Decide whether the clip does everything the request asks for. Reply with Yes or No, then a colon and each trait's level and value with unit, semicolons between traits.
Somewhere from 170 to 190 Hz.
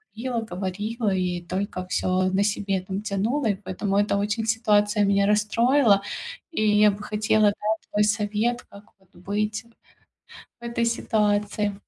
No: high, 210 Hz